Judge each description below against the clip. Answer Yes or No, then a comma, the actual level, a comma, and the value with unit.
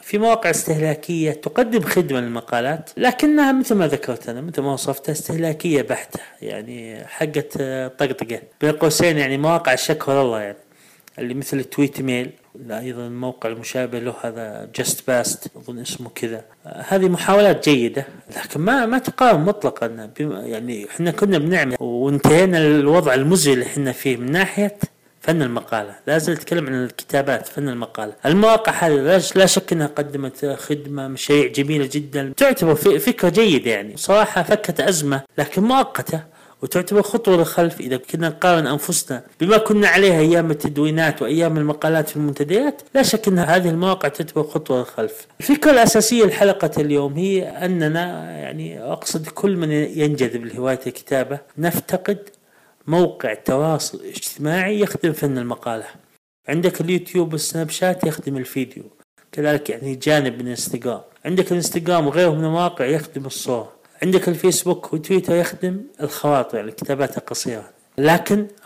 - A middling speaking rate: No, fast, 140 wpm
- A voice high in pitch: No, medium, 155 Hz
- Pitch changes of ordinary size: Yes, average, 5.0 semitones